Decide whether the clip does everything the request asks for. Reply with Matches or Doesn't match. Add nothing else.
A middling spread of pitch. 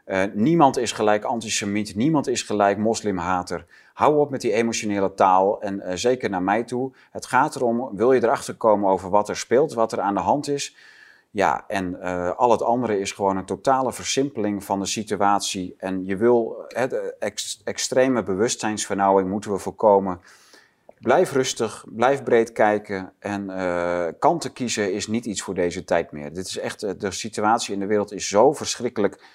Matches